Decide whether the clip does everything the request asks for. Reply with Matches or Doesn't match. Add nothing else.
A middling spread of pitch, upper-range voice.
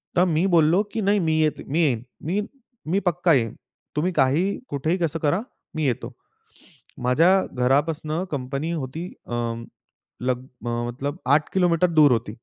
Doesn't match